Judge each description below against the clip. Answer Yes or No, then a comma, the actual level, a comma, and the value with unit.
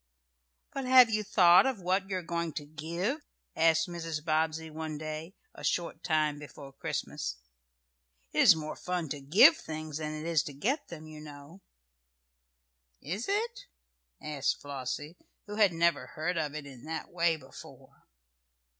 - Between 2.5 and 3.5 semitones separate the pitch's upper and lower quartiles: Yes, average, 2.9 semitones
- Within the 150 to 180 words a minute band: Yes, average, 160 wpm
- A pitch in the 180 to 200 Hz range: No, medium, 160 Hz